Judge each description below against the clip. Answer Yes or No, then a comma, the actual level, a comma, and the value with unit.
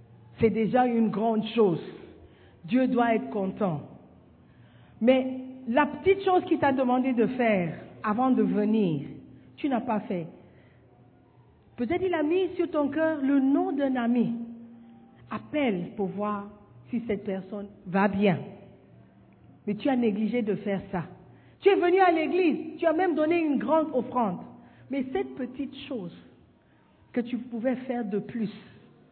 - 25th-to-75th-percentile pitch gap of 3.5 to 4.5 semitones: No, average, 5.3 semitones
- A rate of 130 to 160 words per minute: Yes, average, 150 wpm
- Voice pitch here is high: Yes, high, 235 Hz